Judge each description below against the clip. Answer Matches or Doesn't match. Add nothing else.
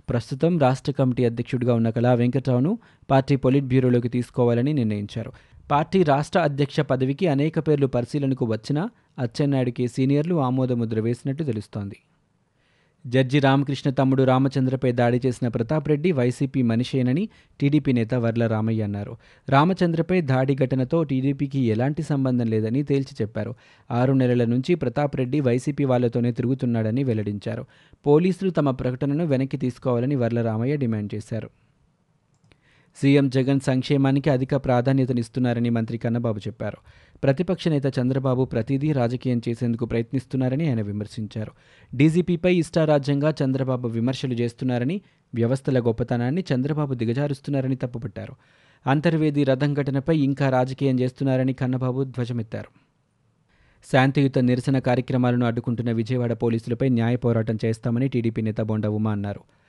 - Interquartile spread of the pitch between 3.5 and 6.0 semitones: Doesn't match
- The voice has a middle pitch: Doesn't match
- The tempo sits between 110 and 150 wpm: Matches